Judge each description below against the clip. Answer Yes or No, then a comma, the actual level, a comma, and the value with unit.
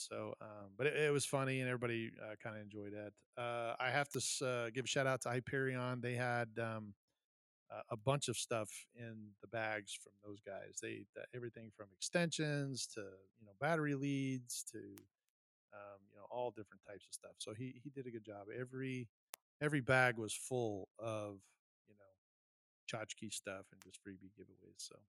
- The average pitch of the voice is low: Yes, low, 120 Hz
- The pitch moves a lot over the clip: No, average, 3.8 semitones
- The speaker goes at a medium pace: Yes, average, 190 wpm